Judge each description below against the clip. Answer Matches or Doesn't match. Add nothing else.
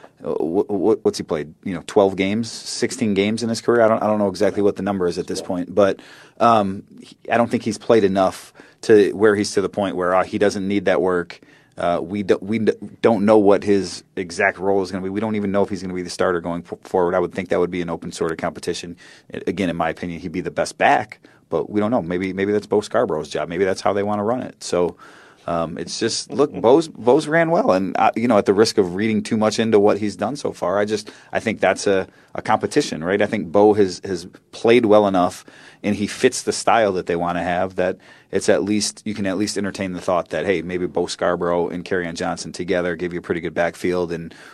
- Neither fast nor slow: Doesn't match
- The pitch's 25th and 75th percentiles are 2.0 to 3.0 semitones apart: Matches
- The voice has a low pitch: Matches